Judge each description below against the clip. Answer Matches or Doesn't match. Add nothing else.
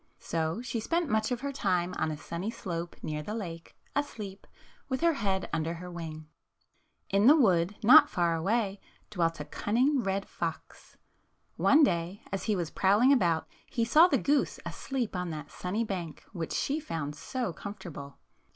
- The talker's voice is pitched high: Matches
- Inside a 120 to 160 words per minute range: Doesn't match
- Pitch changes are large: Matches